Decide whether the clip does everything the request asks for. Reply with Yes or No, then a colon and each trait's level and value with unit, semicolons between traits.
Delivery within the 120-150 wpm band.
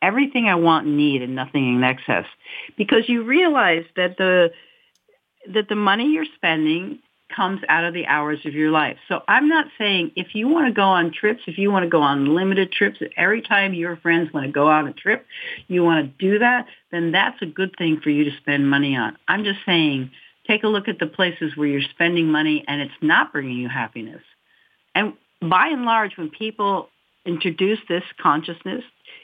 No: fast, 205 wpm